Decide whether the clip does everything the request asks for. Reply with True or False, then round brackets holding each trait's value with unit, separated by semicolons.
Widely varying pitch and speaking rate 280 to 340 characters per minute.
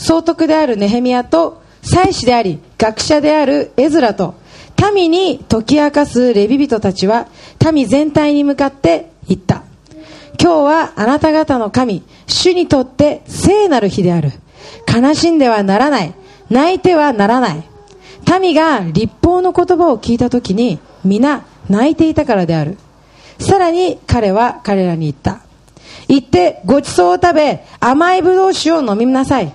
True (7.8 semitones; 290 characters per minute)